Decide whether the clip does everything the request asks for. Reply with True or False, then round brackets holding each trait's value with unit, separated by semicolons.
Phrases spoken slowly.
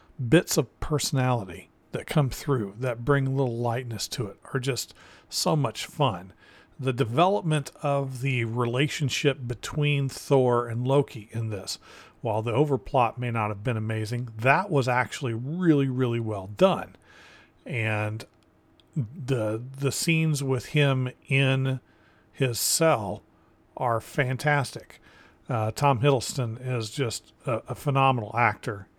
True (130 wpm)